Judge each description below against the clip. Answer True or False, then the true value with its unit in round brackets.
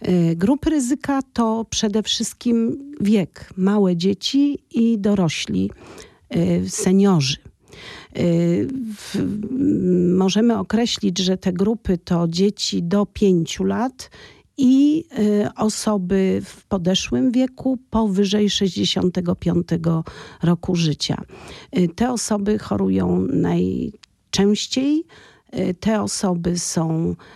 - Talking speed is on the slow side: True (80 wpm)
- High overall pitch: True (200 Hz)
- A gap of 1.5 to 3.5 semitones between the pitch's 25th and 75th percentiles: False (4.3 semitones)